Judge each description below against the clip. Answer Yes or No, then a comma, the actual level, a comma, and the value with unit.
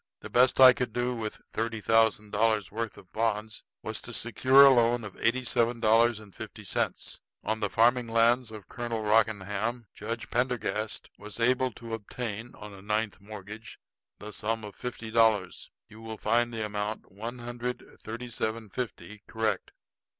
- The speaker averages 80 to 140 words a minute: No, average, 175 wpm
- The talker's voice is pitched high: No, low, 115 Hz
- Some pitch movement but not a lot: No, narrow, 1.9 semitones